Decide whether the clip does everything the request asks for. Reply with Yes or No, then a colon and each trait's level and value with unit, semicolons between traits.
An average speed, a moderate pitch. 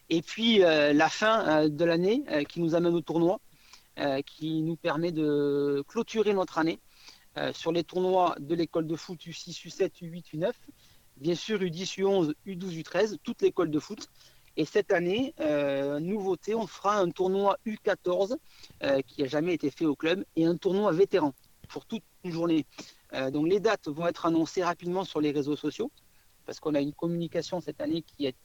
Yes: average, 190 wpm; medium, 170 Hz